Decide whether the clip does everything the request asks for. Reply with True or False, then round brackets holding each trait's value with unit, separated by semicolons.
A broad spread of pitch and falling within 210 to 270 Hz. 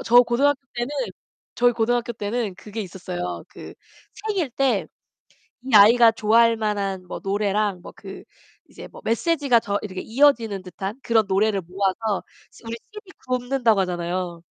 False (3.9 semitones; 220 Hz)